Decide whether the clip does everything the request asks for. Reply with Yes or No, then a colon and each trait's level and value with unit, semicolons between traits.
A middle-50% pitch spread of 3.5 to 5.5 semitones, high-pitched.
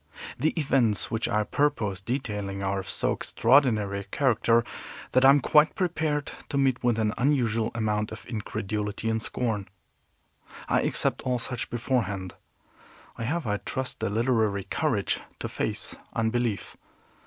No: average, 3.9 semitones; low, 115 Hz